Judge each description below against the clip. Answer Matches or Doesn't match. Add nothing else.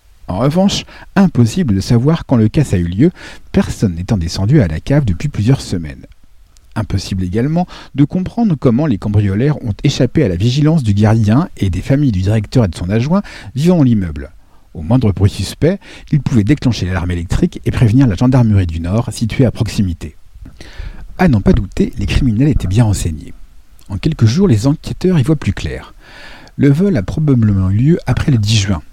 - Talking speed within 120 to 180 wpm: Doesn't match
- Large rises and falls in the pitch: Matches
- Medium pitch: Doesn't match